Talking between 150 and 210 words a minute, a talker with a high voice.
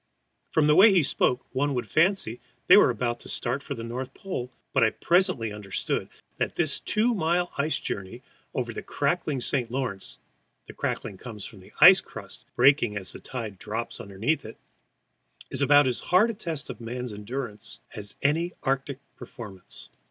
No: average, 175 wpm; low, 130 Hz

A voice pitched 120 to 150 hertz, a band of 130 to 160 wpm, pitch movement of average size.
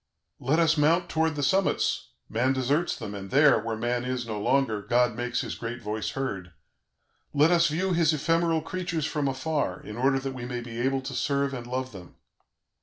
No: low, 135 Hz; average, 195 wpm; average, 4.6 semitones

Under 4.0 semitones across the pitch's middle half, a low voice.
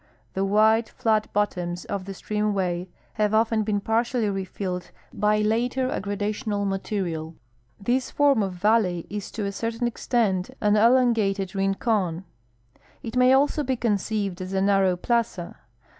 No: average, 2.9 semitones; high, 210 Hz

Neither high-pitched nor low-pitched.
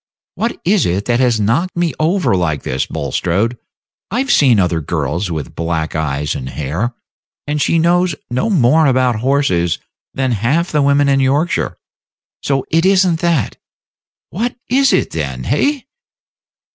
No: low, 130 Hz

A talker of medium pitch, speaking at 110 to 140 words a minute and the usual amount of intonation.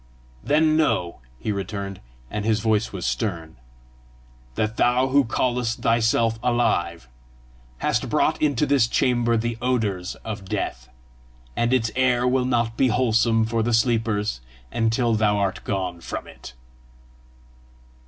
No: low, 115 Hz; slow, 135 wpm; average, 3.0 semitones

